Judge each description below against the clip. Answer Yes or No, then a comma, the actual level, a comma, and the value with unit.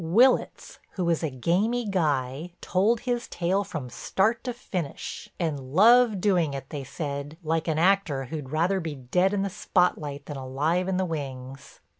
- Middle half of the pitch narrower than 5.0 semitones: No, wide, 5.4 semitones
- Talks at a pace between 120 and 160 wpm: No, average, 170 wpm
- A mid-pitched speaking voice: Yes, medium, 165 Hz